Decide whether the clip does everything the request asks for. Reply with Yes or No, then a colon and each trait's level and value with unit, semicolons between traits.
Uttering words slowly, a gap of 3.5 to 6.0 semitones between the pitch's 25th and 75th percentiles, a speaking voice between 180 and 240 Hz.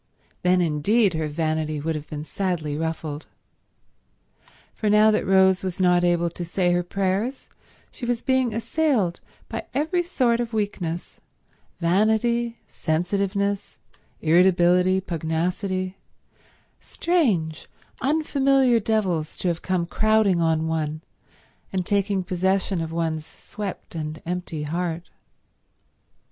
Yes: slow, 115 wpm; average, 4.6 semitones; medium, 185 Hz